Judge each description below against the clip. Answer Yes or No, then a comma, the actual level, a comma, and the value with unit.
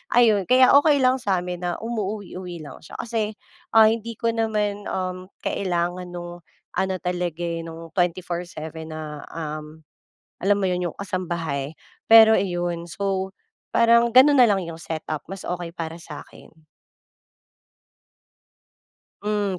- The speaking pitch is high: No, medium, 180 Hz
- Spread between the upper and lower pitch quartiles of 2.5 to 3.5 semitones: No, average, 3.9 semitones